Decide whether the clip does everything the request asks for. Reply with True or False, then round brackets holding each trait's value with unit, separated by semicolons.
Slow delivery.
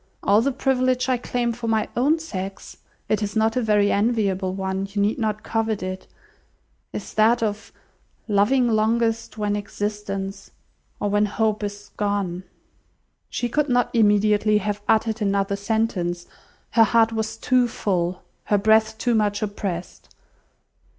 False (145 wpm)